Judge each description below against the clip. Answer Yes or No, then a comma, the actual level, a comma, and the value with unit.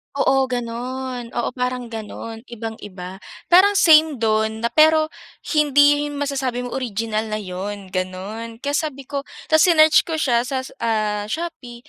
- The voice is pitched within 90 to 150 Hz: No, high, 245 Hz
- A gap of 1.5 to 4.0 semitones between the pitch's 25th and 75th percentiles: No, average, 4.8 semitones